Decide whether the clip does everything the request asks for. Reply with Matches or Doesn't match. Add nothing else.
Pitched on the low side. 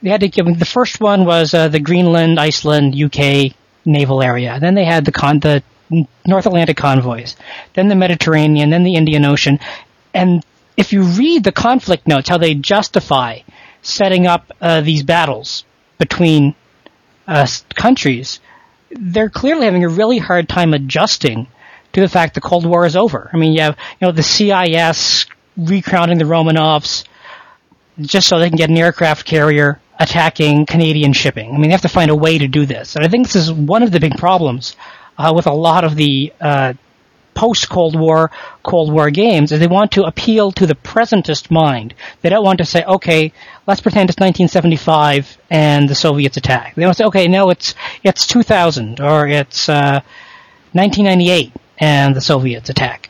Doesn't match